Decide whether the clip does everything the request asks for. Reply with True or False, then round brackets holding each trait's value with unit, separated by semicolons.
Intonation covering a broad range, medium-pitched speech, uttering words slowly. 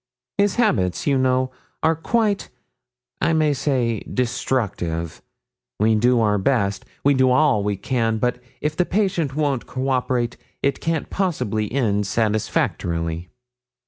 False (5.7 semitones; 125 Hz; 130 wpm)